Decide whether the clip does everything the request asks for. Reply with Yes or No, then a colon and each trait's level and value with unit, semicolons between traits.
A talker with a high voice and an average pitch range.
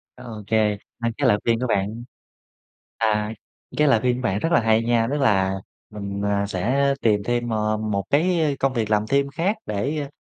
No: low, 115 Hz; average, 4.8 semitones